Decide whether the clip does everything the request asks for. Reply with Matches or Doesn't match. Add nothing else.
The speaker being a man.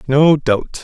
Matches